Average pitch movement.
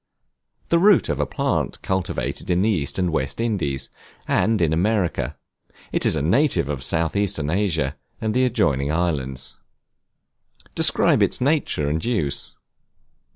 No: wide, 6.9 semitones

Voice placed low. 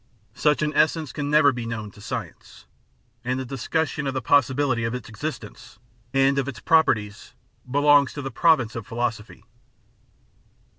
Yes: low, 130 Hz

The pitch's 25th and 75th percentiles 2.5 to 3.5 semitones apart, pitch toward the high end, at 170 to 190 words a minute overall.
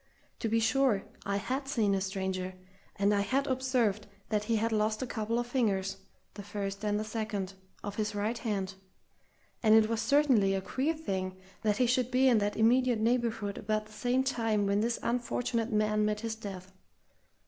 Yes: average, 2.9 semitones; high, 215 Hz; average, 180 wpm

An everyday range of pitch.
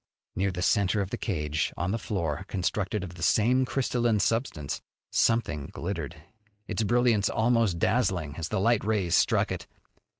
Yes: average, 5.0 semitones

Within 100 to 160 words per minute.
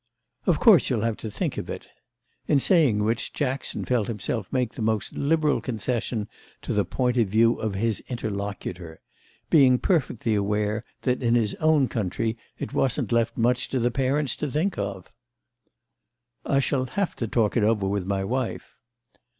No: average, 170 wpm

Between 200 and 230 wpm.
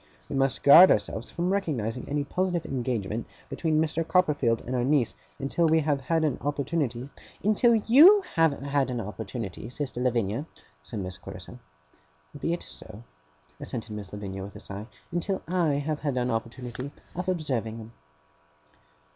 No: average, 160 wpm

